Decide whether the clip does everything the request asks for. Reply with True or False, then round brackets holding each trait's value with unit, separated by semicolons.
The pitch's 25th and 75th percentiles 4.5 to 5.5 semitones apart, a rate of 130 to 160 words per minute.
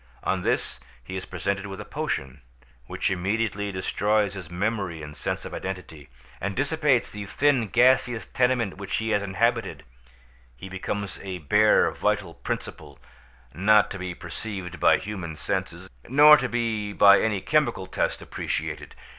False (3.7 semitones; 150 wpm)